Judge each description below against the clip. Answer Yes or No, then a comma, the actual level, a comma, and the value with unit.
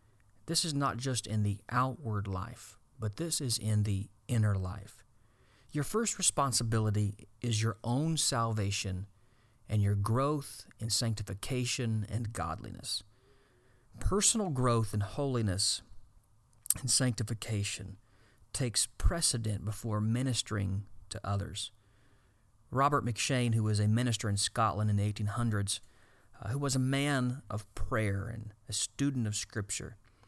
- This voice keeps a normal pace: No, slow, 125 wpm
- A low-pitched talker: Yes, low, 110 Hz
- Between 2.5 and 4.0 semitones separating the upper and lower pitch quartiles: Yes, average, 3.2 semitones